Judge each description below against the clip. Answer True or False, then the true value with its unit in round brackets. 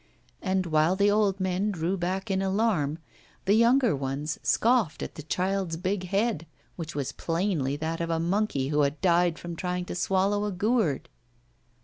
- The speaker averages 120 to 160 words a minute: False (170 wpm)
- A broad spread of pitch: False (3.8 semitones)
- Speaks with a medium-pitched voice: True (180 Hz)